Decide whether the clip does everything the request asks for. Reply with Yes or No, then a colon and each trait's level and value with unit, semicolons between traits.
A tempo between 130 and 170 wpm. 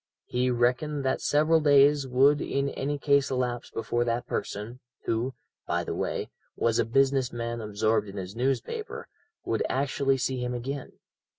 Yes: average, 160 wpm